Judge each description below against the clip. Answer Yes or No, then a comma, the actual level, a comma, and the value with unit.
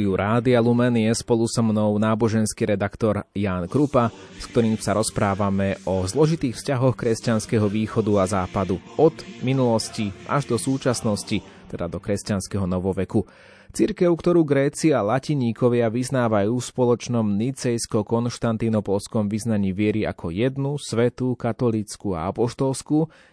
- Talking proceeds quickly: No, average, 120 wpm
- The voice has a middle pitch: No, low, 115 Hz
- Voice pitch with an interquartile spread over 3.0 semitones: Yes, average, 3.7 semitones